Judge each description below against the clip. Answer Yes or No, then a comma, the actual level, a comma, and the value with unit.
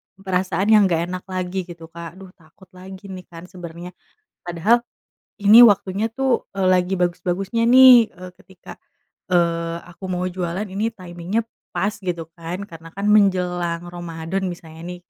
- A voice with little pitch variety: Yes, narrow, 2.1 semitones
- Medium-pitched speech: Yes, medium, 180 Hz